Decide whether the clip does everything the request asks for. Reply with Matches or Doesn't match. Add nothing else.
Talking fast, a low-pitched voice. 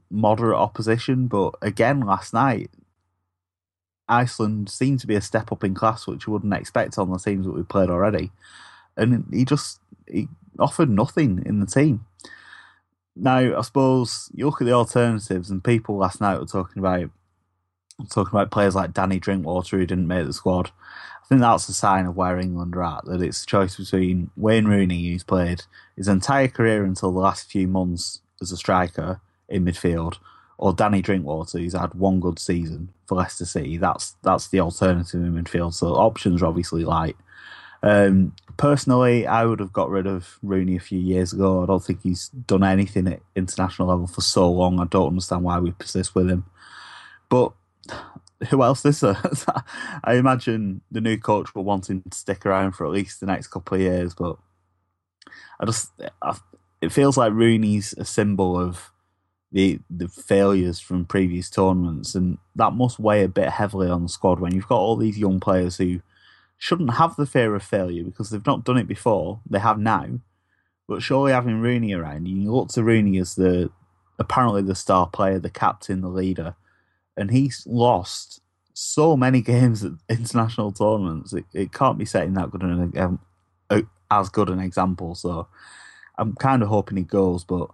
Doesn't match